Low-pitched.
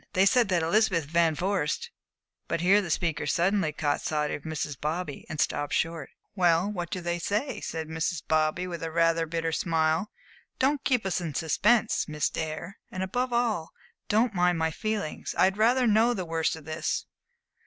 No: medium, 170 Hz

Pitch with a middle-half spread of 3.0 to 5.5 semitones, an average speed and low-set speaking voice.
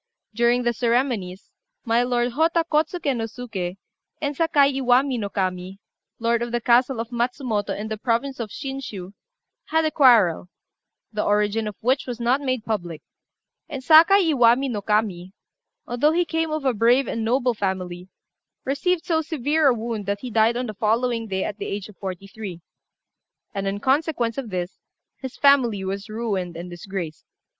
No: average, 4.8 semitones; average, 170 wpm; high, 235 Hz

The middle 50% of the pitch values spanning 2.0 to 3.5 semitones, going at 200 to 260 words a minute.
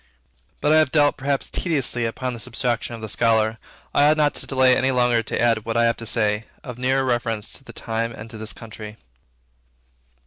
Yes: average, 2.8 semitones; fast, 205 wpm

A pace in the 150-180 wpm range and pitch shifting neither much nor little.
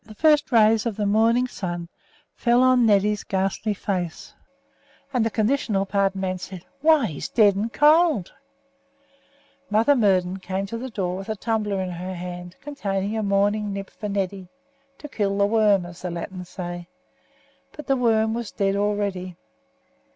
Yes: average, 165 wpm; average, 3.1 semitones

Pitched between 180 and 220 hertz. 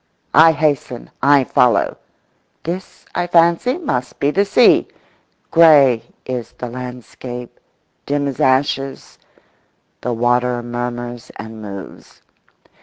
No: low, 130 Hz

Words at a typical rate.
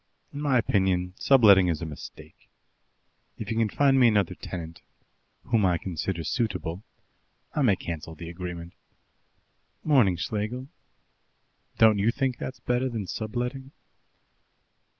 No: slow, 130 wpm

